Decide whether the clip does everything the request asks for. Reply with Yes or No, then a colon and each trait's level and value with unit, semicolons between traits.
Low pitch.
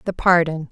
No: medium, 170 Hz